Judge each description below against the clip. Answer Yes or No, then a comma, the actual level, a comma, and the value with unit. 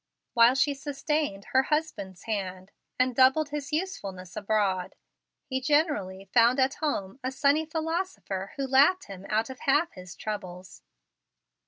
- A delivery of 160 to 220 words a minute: No, average, 140 wpm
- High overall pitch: Yes, very high, 260 Hz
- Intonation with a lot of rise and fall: Yes, wide, 7.0 semitones